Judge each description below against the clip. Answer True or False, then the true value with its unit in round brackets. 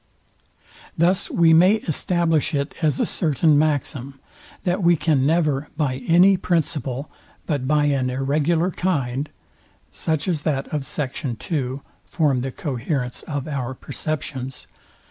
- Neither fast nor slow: False (105 wpm)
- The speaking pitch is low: False (150 Hz)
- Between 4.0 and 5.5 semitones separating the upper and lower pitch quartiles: False (3.4 semitones)